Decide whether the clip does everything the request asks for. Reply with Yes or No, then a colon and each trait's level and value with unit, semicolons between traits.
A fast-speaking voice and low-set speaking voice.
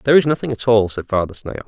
Yes: fast, 285 wpm; low, 115 Hz